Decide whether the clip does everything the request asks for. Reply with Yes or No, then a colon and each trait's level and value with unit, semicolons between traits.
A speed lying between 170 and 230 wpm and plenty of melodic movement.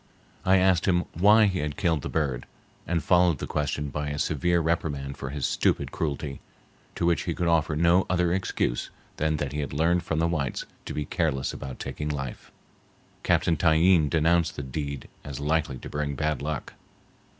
No: average, 185 wpm; average, 3.0 semitones